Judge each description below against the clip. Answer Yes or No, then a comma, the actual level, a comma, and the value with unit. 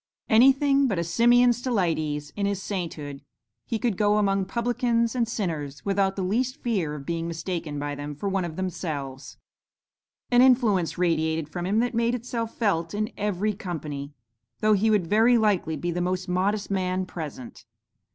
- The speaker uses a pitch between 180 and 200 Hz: Yes, high, 190 Hz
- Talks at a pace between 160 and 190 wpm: Yes, average, 170 wpm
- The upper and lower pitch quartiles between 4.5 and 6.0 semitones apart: Yes, wide, 5.5 semitones